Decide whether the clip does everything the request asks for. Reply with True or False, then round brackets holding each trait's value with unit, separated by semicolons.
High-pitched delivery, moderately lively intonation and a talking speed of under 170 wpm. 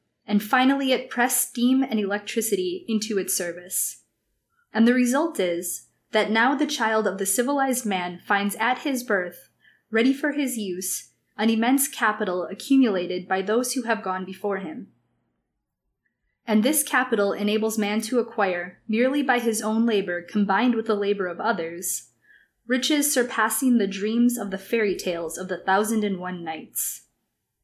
True (215 Hz; 4.6 semitones; 160 wpm)